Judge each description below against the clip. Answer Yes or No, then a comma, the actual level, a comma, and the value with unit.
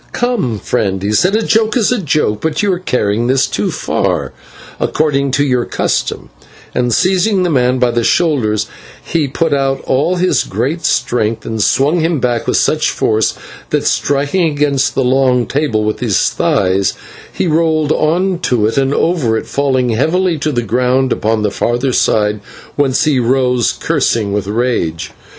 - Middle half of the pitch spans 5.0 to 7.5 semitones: Yes, wide, 5.4 semitones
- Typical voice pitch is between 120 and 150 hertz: Yes, low, 135 Hz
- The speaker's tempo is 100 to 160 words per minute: No, average, 170 wpm